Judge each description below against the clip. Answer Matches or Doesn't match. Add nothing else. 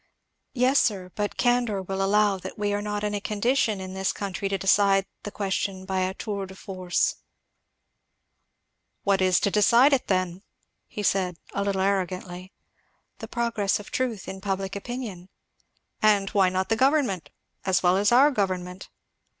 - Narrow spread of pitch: Matches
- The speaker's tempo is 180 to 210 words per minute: Doesn't match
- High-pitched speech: Matches